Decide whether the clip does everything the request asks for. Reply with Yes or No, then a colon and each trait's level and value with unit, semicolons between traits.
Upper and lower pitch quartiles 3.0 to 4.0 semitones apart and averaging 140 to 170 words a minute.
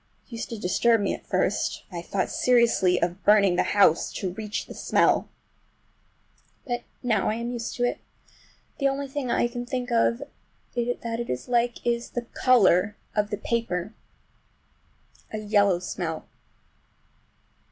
Yes: average, 3.7 semitones; average, 150 wpm